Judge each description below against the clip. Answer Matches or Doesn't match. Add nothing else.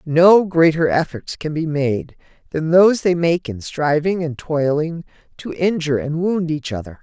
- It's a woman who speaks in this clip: Matches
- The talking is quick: Doesn't match